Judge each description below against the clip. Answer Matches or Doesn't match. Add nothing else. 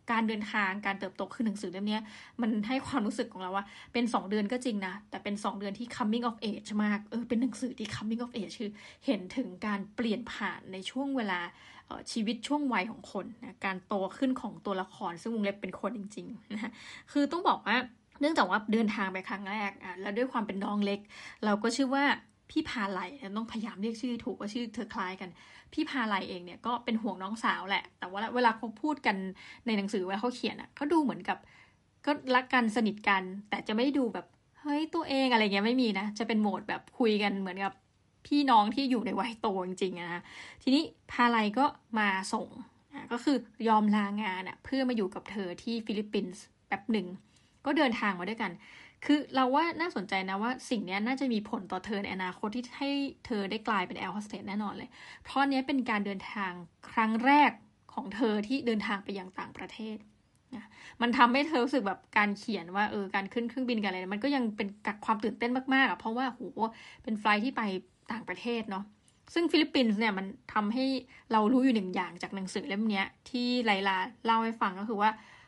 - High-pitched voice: Matches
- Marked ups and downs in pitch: Doesn't match